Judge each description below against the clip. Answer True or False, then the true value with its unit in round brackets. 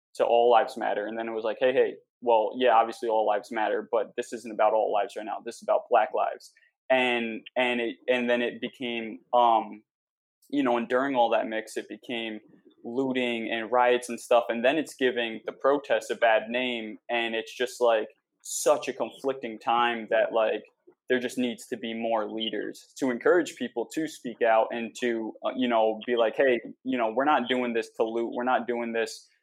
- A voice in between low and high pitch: False (120 Hz)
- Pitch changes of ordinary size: False (1.9 semitones)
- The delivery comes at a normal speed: False (210 wpm)